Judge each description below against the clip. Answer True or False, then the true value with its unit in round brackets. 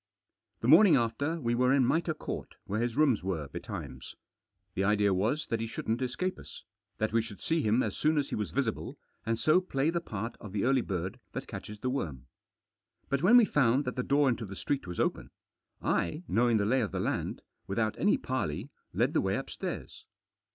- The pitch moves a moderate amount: True (5.0 semitones)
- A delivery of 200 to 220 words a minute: True (205 wpm)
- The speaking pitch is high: False (120 Hz)